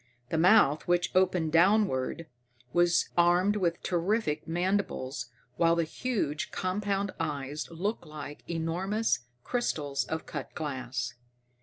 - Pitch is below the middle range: No, medium, 170 Hz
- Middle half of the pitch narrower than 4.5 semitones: Yes, average, 4.1 semitones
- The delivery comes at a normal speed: No, slow, 115 wpm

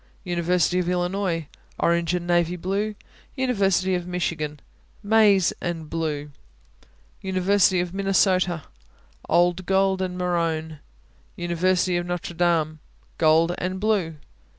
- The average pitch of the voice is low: No, medium, 180 Hz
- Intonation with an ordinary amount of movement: No, narrow, 1.9 semitones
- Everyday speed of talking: No, slow, 110 wpm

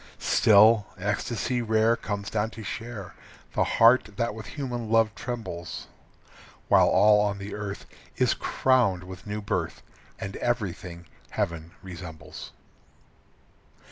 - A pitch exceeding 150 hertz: No, low, 105 Hz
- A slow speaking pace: Yes, slow, 120 wpm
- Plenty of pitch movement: No, average, 3.2 semitones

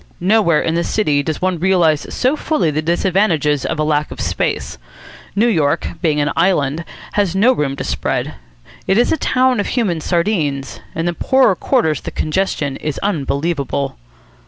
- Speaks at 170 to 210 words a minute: Yes, average, 175 wpm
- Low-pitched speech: No, medium, 170 Hz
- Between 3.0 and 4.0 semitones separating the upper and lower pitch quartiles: No, average, 5.1 semitones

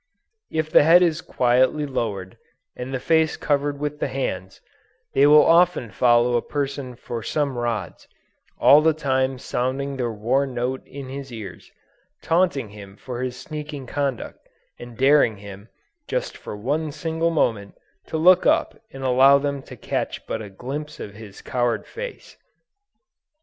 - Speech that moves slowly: No, average, 155 wpm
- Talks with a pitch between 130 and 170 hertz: Yes, low, 135 Hz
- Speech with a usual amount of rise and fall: Yes, average, 3.8 semitones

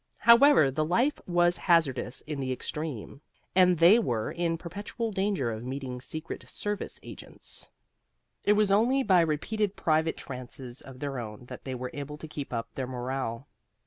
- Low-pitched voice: No, medium, 155 Hz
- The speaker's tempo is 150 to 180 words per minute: Yes, average, 165 wpm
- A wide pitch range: Yes, wide, 6.5 semitones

